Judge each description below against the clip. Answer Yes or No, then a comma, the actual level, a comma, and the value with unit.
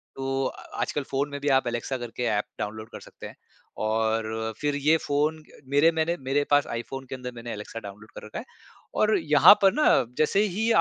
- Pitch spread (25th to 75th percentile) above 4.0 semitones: Yes, average, 4.8 semitones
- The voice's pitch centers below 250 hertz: Yes, low, 135 Hz